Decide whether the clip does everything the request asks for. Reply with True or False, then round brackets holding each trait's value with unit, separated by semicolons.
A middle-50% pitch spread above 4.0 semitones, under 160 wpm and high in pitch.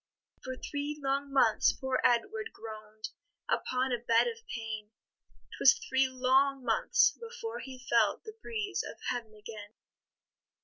True (4.7 semitones; 135 wpm; 260 Hz)